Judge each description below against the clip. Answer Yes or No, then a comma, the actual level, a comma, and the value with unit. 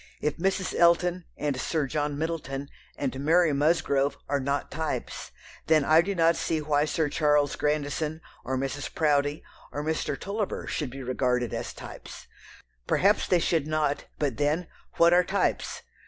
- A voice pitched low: No, medium, 150 Hz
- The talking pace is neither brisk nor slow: Yes, average, 155 wpm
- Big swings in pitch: No, average, 2.7 semitones